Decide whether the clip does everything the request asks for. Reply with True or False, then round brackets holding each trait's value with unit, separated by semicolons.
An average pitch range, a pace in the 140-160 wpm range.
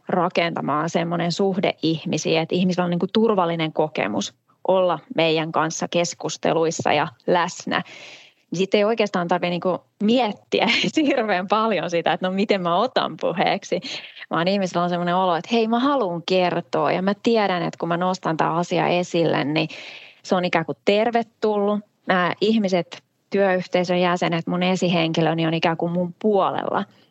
True (3.0 semitones; 155 wpm)